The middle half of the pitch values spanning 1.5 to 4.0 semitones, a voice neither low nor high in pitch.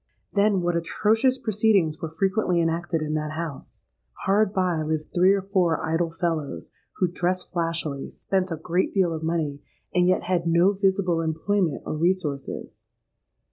Yes: average, 2.9 semitones; medium, 175 Hz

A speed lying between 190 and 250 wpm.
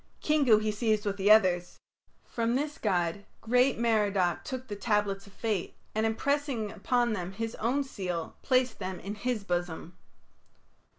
No: average, 155 wpm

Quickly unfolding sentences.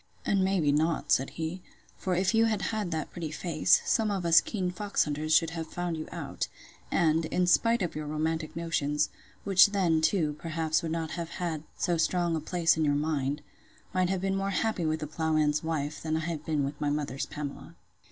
Yes: fast, 210 wpm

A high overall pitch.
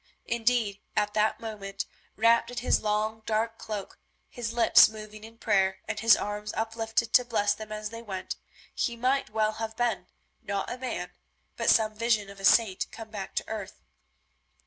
Yes: high, 220 Hz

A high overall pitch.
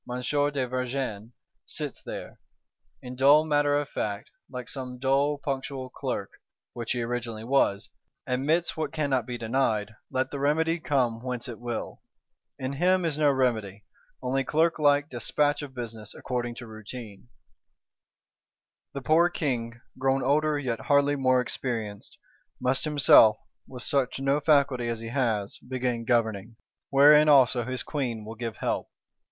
No: low, 130 Hz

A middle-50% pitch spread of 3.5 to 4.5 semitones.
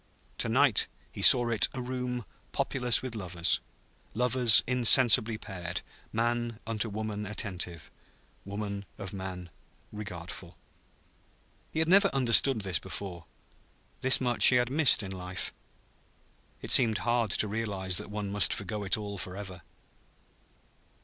Yes: average, 4.2 semitones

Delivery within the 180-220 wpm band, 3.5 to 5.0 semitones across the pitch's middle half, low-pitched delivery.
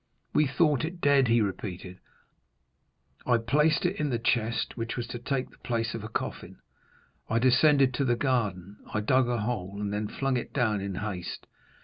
Yes: average, 190 wpm; average, 3.9 semitones; low, 120 Hz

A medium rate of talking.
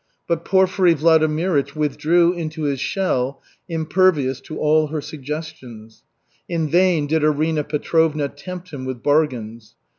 No: slow, 125 wpm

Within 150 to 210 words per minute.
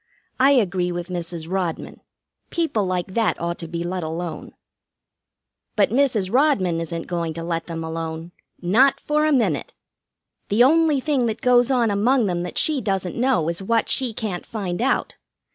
Yes: average, 170 wpm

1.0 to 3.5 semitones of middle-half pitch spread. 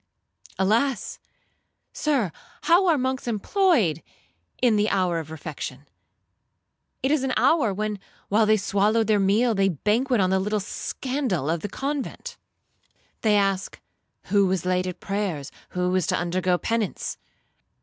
No: average, 4.9 semitones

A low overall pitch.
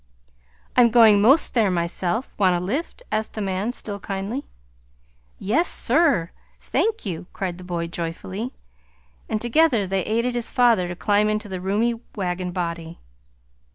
No: high, 205 Hz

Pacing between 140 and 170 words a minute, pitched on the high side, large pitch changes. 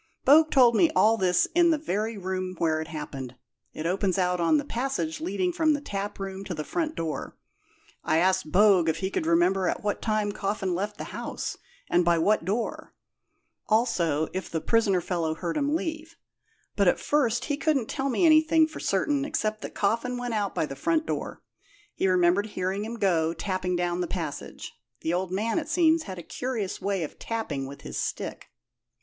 No: average, 195 wpm; high, 195 Hz; wide, 5.9 semitones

